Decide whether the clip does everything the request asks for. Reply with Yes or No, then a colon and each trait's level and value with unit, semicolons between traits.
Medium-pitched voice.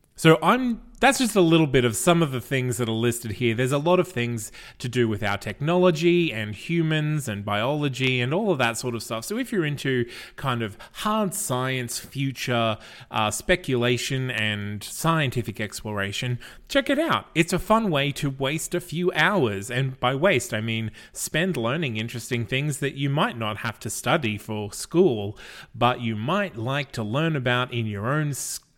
No: low, 130 Hz